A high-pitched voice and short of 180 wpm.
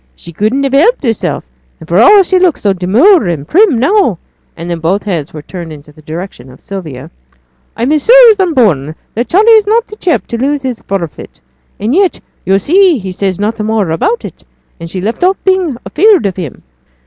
No: high, 225 Hz; fast, 205 wpm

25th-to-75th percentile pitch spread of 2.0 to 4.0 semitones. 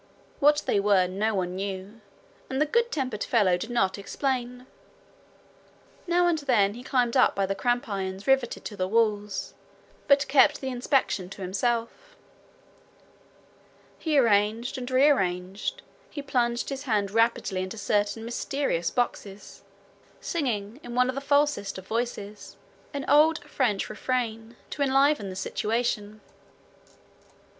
No: average, 4.9 semitones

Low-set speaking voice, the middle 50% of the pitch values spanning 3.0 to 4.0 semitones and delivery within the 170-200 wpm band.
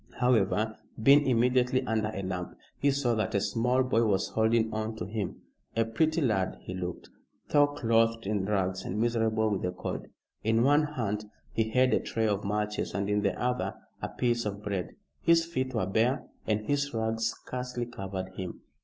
Yes: low, 110 Hz; average, 3.3 semitones; average, 185 wpm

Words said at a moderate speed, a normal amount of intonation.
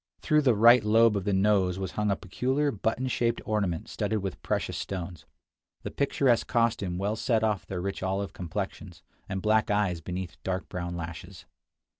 Yes: average, 175 wpm; average, 3.3 semitones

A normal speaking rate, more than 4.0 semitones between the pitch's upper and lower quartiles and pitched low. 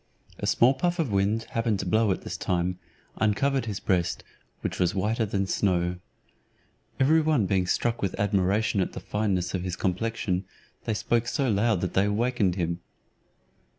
No: average, 170 wpm; average, 3.7 semitones; low, 100 Hz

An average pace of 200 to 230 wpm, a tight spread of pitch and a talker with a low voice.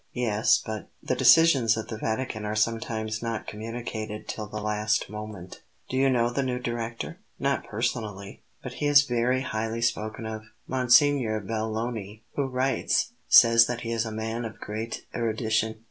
No: average, 160 wpm; narrow, 2.0 semitones; low, 115 Hz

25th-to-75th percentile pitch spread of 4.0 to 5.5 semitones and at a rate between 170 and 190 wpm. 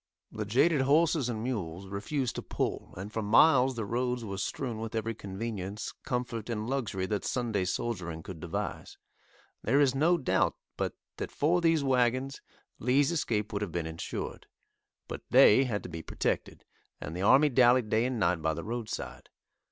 Yes: average, 4.6 semitones; average, 175 wpm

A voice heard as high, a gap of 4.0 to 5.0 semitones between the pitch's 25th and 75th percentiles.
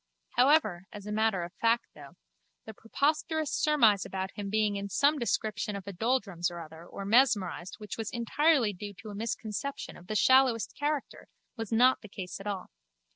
Yes: high, 215 Hz; average, 4.3 semitones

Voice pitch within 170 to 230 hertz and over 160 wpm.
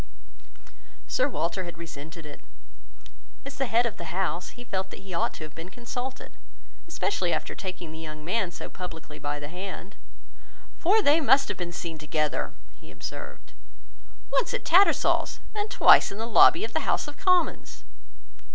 Yes: high, 190 Hz; average, 170 wpm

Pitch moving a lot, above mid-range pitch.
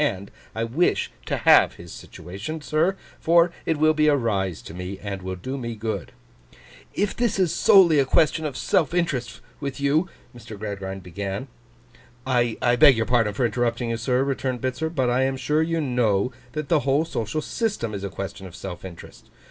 No: wide, 7.0 semitones; low, 125 Hz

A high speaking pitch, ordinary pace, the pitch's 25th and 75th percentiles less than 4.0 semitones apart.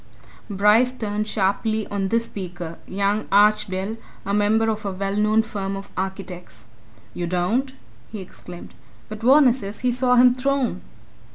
Yes: high, 210 Hz; average, 150 wpm; average, 2.8 semitones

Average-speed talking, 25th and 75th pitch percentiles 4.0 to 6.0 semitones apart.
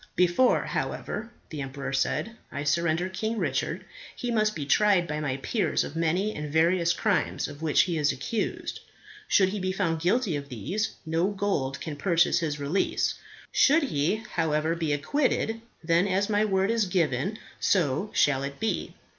Yes: average, 170 wpm; wide, 5.5 semitones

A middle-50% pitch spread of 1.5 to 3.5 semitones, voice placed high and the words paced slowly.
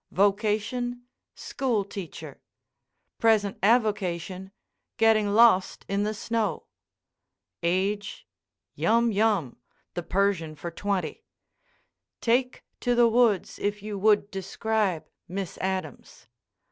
Yes: average, 2.8 semitones; high, 205 Hz; slow, 95 wpm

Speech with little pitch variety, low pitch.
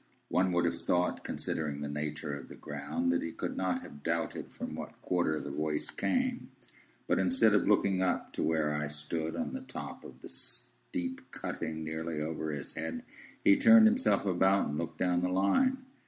No: average, 4.6 semitones; very low, 85 Hz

